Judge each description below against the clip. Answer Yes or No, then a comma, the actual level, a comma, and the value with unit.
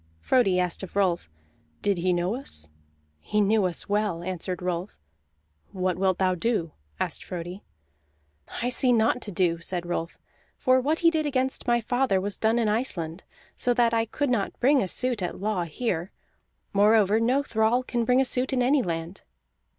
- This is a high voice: Yes, high, 210 Hz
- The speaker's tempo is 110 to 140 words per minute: No, average, 180 wpm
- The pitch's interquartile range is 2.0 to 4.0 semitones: No, average, 5.3 semitones